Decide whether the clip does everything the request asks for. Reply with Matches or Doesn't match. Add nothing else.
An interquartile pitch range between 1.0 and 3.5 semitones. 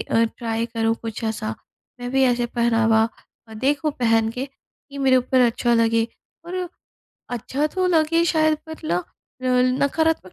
Doesn't match